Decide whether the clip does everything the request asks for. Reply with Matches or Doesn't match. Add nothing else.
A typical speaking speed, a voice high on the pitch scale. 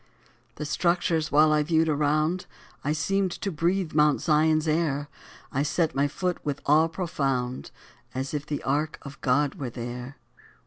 Doesn't match